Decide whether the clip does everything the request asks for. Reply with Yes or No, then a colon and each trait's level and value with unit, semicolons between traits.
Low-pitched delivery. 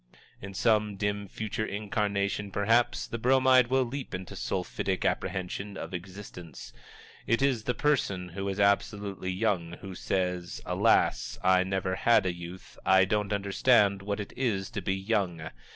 Yes: low, 100 Hz